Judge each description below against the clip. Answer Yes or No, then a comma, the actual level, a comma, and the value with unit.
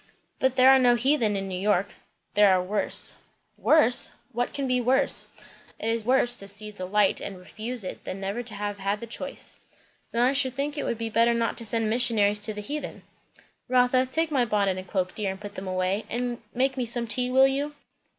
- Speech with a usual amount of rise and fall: Yes, average, 3.9 semitones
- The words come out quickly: Yes, fast, 220 wpm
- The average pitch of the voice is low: No, high, 230 Hz